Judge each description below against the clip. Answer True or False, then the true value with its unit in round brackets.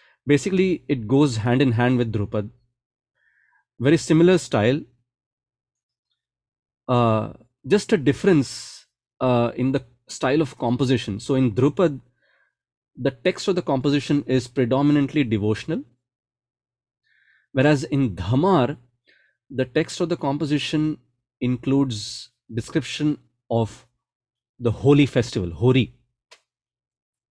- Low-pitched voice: True (130 Hz)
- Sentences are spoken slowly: True (105 wpm)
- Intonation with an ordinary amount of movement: True (3.1 semitones)